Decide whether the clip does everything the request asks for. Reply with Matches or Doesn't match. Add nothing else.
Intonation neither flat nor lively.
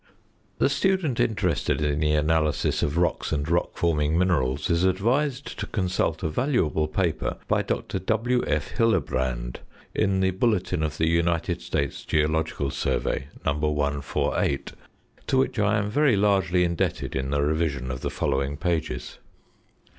Matches